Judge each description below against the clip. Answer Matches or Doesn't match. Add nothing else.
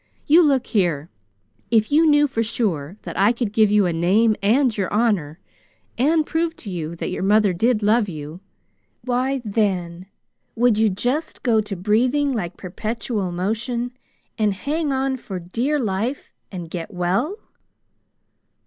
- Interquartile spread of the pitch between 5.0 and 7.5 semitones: Matches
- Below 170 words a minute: Matches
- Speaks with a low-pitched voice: Doesn't match